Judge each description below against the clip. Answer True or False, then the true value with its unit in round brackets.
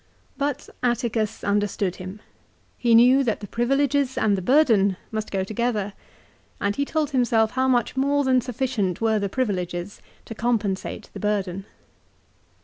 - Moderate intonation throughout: True (4.2 semitones)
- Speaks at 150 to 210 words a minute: False (140 wpm)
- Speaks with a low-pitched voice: False (225 Hz)